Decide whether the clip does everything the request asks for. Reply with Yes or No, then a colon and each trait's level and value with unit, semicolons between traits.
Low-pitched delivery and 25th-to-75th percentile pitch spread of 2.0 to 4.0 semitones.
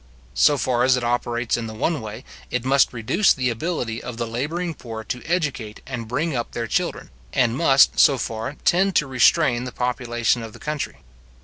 Yes: low, 125 Hz; average, 3.6 semitones